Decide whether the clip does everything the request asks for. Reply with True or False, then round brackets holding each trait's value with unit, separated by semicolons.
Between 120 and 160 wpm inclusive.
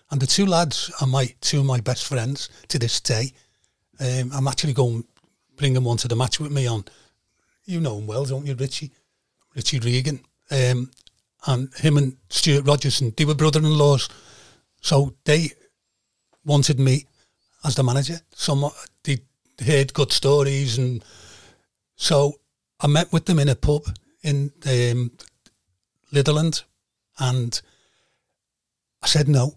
True (150 wpm)